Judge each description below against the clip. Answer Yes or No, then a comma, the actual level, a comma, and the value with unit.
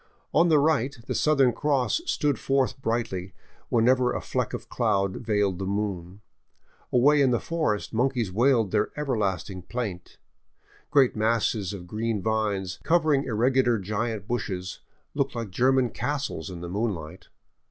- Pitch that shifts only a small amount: No, average, 5.0 semitones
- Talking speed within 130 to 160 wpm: Yes, average, 145 wpm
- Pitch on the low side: Yes, low, 115 Hz